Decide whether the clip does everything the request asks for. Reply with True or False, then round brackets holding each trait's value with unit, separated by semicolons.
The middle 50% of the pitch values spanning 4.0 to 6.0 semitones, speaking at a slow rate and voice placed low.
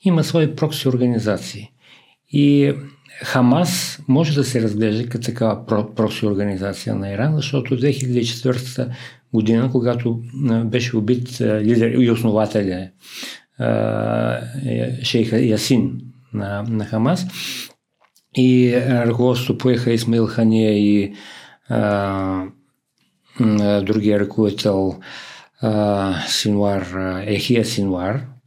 False (3.4 semitones; 80 wpm; 115 Hz)